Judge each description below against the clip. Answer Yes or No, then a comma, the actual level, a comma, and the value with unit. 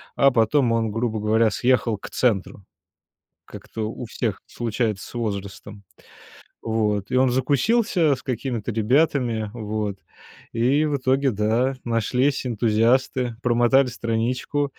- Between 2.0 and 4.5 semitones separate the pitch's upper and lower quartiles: Yes, average, 3.1 semitones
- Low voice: Yes, low, 120 Hz